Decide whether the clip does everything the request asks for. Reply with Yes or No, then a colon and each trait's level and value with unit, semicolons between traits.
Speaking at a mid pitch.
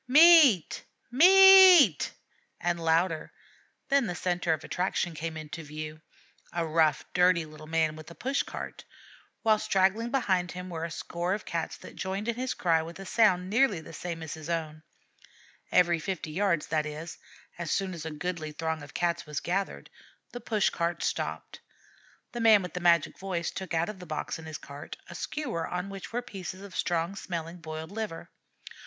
Yes: medium, 175 Hz